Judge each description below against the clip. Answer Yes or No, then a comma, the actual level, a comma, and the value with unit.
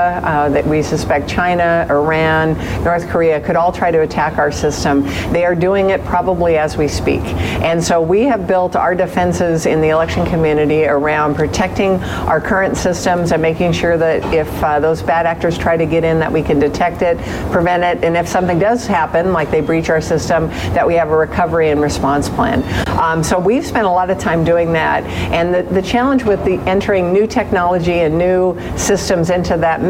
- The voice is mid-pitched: Yes, medium, 170 Hz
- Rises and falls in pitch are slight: Yes, narrow, 2.3 semitones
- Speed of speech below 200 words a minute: No, fast, 205 wpm